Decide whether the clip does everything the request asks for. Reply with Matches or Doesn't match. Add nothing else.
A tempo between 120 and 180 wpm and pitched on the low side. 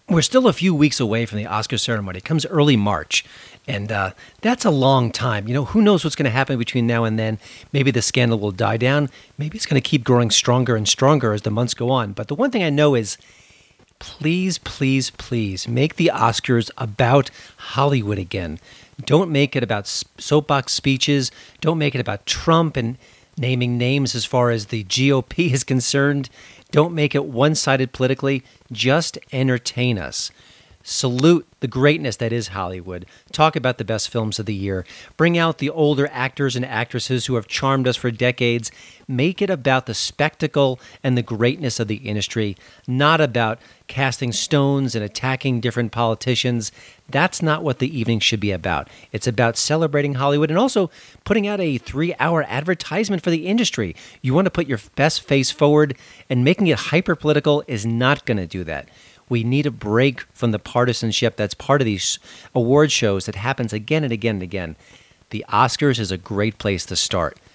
Doesn't match